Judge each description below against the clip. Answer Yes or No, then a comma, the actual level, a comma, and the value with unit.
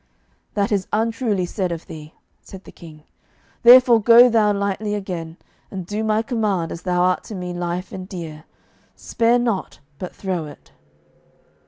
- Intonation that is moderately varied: Yes, average, 3.8 semitones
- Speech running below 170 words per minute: Yes, average, 160 wpm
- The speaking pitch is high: Yes, high, 195 Hz